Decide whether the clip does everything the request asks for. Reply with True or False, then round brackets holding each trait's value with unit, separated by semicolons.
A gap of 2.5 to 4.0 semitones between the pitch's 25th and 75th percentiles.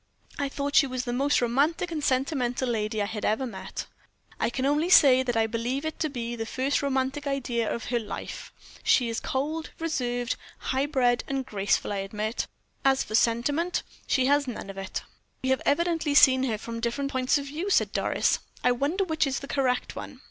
True (3.2 semitones)